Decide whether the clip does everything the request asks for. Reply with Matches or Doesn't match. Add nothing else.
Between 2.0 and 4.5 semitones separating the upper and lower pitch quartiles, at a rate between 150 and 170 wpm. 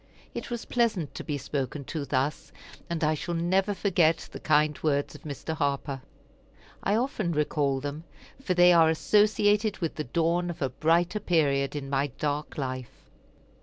Matches